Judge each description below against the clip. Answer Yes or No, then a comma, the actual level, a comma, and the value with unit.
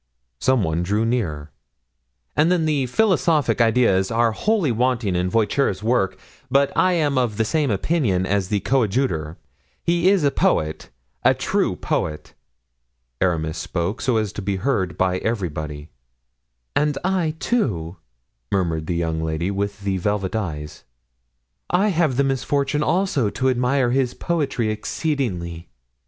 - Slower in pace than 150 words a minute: Yes, average, 140 wpm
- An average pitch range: No, wide, 7.2 semitones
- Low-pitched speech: Yes, low, 115 Hz